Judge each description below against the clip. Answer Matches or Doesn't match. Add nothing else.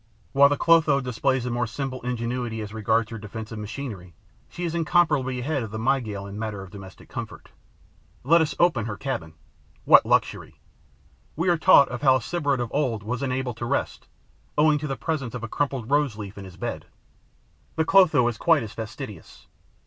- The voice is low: Matches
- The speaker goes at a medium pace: Matches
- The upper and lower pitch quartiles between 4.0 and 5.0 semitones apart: Matches